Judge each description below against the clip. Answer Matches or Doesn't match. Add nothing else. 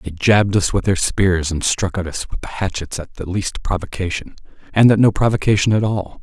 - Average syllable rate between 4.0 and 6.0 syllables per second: Matches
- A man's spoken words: Matches